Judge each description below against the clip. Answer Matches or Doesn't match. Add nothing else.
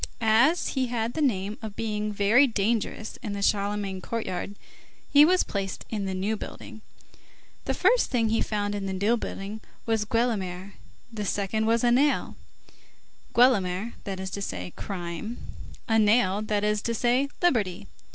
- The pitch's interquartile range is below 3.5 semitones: Matches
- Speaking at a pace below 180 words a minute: Matches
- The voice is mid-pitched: Doesn't match